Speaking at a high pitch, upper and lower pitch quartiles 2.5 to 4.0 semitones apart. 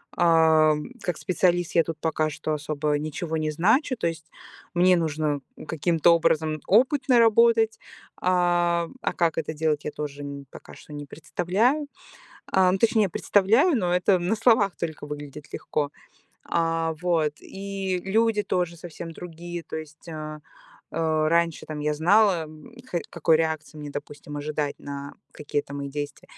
No: medium, 165 Hz; average, 3.1 semitones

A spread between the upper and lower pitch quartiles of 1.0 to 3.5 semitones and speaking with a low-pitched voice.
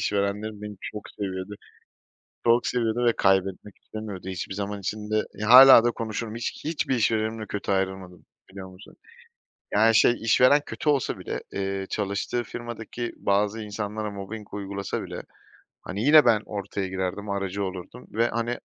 Yes: average, 2.7 semitones; low, 105 Hz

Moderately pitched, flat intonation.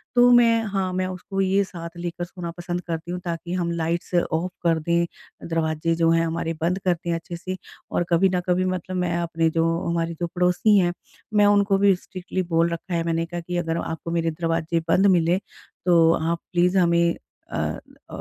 Yes: medium, 175 Hz; narrow, 1.7 semitones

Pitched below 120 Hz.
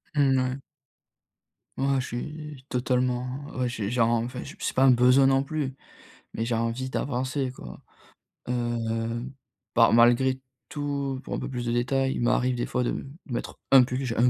No: low, 125 Hz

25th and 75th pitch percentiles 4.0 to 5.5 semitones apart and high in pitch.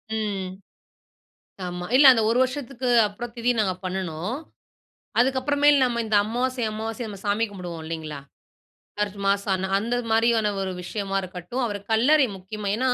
Yes: average, 4.4 semitones; high, 215 Hz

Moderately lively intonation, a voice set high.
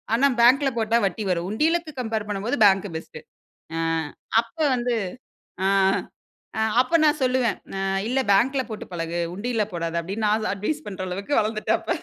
Yes: average, 4.6 semitones; high, 220 Hz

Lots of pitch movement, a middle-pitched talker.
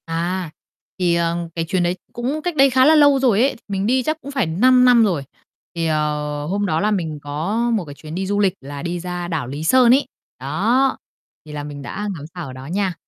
Yes: wide, 7.4 semitones; medium, 180 Hz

